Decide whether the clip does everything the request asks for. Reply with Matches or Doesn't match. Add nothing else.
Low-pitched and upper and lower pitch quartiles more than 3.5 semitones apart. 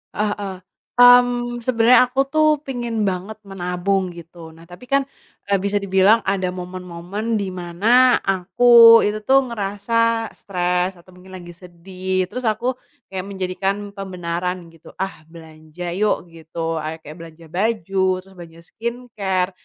Doesn't match